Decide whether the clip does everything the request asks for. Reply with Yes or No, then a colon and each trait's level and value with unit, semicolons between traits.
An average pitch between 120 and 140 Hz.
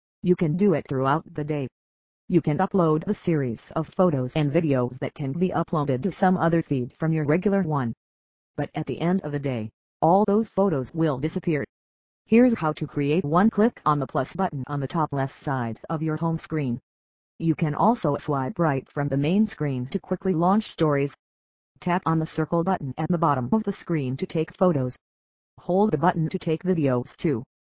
No: medium, 155 Hz